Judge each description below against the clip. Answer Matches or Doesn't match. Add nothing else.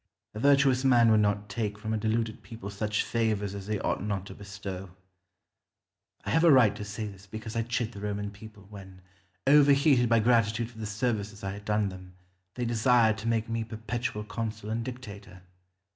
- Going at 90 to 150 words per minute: Doesn't match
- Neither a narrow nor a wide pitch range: Doesn't match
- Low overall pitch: Matches